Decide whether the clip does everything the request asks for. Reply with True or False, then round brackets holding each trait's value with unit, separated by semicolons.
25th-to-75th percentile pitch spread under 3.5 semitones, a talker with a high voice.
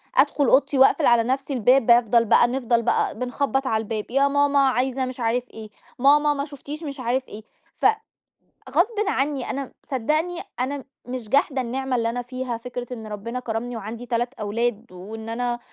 True (2.9 semitones; 250 Hz)